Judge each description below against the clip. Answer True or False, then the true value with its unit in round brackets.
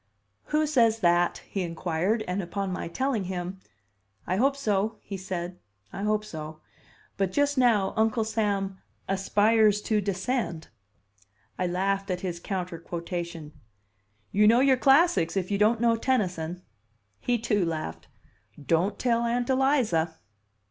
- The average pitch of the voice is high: True (195 Hz)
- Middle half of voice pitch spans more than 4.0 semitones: True (4.4 semitones)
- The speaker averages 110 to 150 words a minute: True (140 wpm)